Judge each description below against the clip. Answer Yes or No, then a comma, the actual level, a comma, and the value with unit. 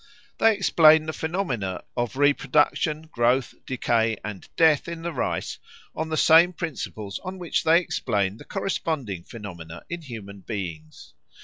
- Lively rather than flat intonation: Yes, wide, 7.8 semitones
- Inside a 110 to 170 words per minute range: Yes, average, 140 wpm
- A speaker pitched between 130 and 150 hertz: Yes, low, 135 Hz